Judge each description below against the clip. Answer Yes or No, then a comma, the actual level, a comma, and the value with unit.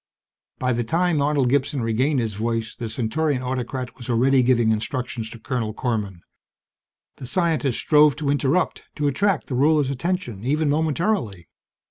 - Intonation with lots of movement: No, average, 4.4 semitones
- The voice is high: No, low, 130 Hz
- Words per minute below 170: Yes, average, 150 wpm